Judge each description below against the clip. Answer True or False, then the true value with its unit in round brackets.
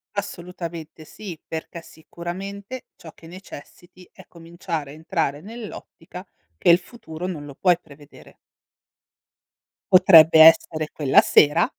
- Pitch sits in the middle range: True (170 Hz)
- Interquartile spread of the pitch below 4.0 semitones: True (2.7 semitones)